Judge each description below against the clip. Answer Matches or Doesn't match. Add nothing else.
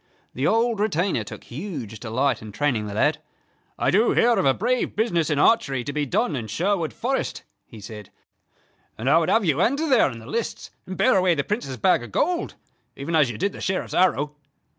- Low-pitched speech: Doesn't match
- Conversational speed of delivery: Doesn't match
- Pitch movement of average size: Doesn't match